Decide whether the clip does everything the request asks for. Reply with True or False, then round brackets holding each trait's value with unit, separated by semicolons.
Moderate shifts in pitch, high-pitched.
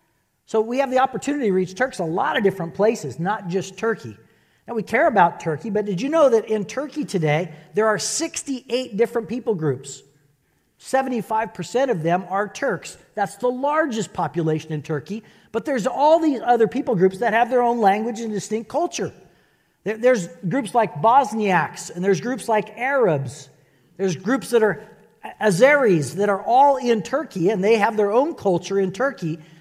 False (5.7 semitones; 215 Hz)